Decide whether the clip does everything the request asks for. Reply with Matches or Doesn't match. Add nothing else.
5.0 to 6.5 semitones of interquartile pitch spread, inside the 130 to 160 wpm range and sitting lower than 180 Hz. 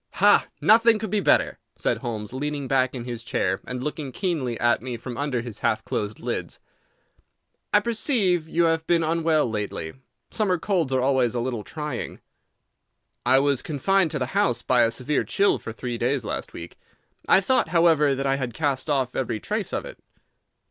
Doesn't match